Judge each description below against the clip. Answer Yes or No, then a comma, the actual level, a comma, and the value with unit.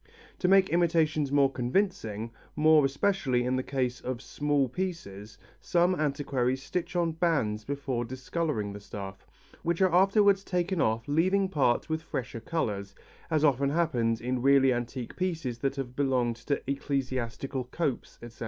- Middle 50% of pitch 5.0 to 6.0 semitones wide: Yes, average, 5.3 semitones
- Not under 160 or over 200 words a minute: No, average, 150 wpm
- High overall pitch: No, medium, 140 Hz